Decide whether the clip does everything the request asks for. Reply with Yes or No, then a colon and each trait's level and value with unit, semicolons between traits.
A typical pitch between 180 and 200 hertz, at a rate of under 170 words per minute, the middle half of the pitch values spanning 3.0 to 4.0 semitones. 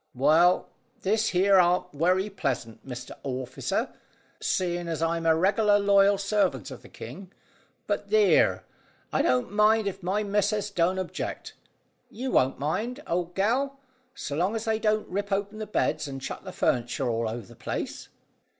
No: medium, 185 Hz; average, 160 wpm; wide, 5.6 semitones